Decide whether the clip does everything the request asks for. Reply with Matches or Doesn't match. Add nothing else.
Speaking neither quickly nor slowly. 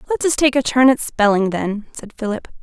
Doesn't match